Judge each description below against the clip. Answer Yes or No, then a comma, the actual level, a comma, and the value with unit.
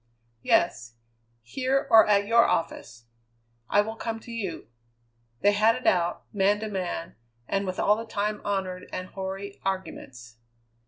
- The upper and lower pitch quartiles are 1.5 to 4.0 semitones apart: Yes, average, 3.0 semitones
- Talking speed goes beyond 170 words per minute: No, average, 150 wpm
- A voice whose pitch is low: No, high, 200 Hz